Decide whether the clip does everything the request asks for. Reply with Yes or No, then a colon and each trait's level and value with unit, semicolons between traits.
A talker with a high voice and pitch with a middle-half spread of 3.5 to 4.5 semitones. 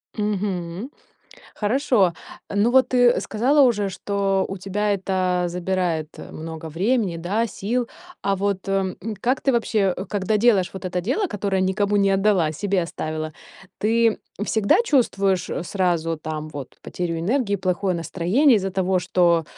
No: high, 195 Hz; average, 3.1 semitones